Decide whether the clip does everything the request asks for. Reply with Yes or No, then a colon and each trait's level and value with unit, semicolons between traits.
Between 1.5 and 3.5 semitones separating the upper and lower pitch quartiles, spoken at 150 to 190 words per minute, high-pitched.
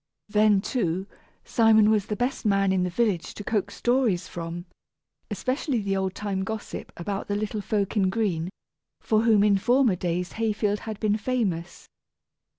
Yes: narrow, 2.6 semitones; average, 160 wpm; high, 205 Hz